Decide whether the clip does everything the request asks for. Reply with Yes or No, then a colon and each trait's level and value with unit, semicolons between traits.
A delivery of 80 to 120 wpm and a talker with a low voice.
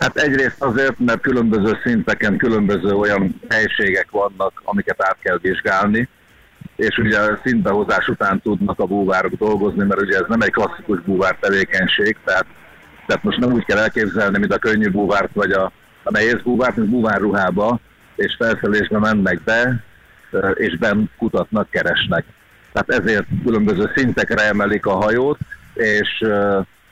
No: average, 140 wpm; low, 105 Hz